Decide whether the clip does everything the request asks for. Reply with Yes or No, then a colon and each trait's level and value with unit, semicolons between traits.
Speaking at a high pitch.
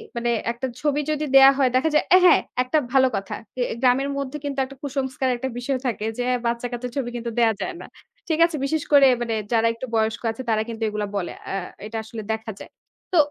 Yes: very high, 250 Hz